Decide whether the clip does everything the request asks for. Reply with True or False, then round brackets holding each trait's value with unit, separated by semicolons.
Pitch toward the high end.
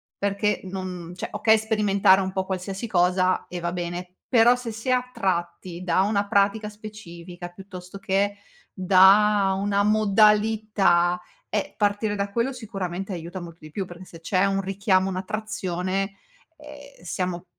True (195 Hz)